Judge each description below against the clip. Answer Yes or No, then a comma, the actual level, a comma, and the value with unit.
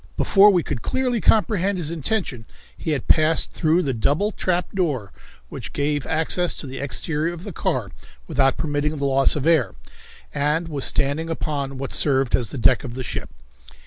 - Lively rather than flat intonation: No, average, 4.1 semitones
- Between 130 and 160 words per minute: No, average, 180 wpm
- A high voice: No, medium, 150 Hz